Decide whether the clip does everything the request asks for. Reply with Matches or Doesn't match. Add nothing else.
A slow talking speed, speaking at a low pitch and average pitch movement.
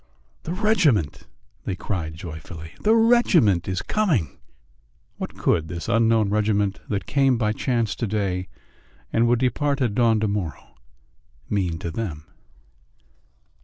Doesn't match